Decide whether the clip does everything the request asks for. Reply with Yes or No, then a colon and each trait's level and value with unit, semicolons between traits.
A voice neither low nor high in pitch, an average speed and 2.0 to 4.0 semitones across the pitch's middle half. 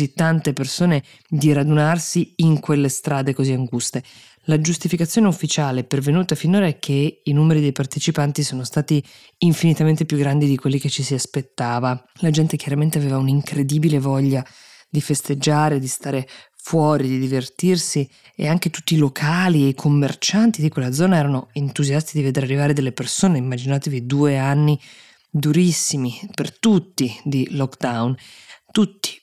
Yes: medium, 145 Hz; average, 145 wpm; average, 2.7 semitones